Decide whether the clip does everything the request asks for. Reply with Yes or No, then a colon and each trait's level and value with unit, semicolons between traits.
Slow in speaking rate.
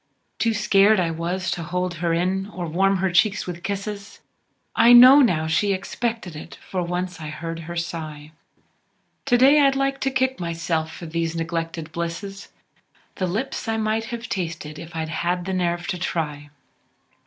No: average, 175 wpm